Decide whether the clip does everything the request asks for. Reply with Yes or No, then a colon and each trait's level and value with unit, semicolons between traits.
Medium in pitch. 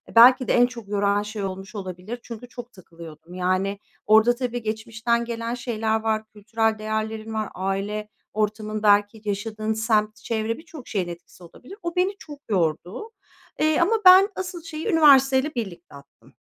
No: high, 220 Hz